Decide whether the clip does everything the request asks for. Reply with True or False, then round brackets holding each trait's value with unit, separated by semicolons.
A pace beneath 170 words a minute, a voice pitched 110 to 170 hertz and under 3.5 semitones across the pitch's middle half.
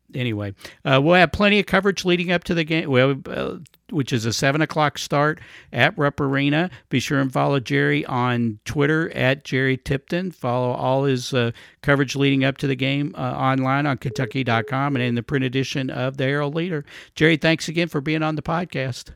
False (200 wpm; 140 Hz; 3.0 semitones)